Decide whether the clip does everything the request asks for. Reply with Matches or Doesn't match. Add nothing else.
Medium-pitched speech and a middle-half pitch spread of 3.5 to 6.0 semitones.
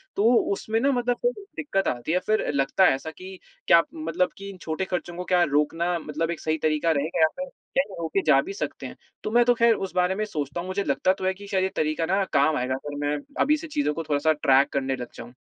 Matches